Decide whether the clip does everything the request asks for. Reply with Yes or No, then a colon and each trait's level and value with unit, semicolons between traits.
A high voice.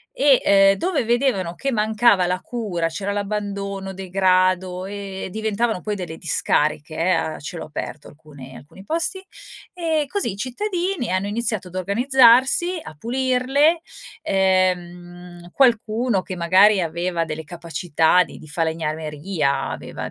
Yes: high, 195 Hz